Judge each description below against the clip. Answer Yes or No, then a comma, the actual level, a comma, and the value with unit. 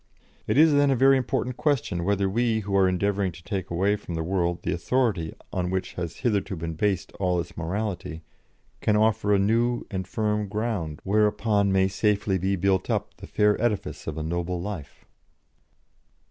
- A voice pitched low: Yes, low, 100 Hz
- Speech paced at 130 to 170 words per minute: No, average, 180 wpm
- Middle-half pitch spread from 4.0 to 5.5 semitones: No, average, 3.2 semitones